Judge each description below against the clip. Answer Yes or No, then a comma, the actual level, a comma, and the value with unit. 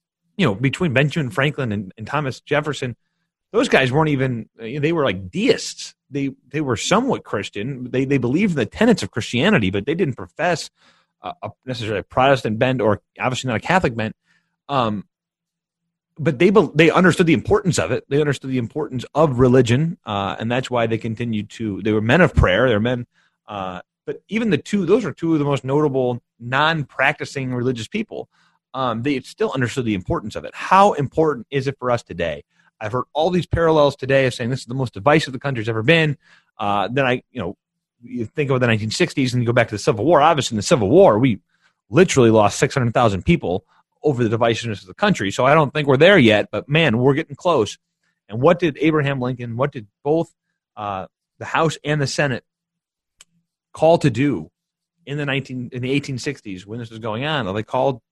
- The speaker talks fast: Yes, fast, 210 wpm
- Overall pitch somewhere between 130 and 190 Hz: Yes, low, 135 Hz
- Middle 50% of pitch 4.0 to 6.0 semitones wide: Yes, average, 4.9 semitones